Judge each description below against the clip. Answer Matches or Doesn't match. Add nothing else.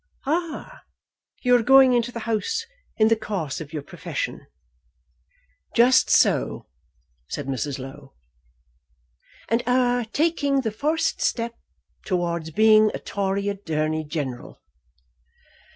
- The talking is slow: Matches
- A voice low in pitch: Doesn't match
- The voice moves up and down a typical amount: Doesn't match